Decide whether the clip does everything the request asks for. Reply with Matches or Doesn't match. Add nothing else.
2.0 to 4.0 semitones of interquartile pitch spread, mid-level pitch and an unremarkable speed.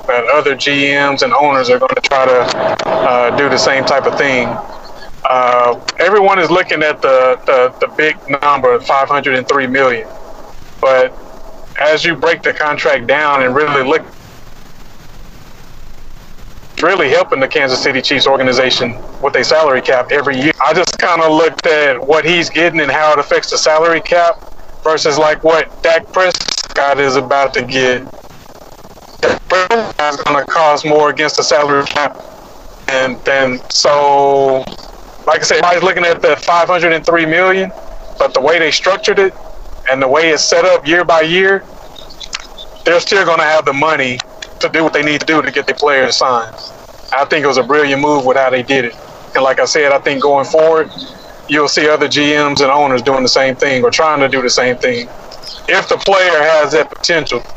Matches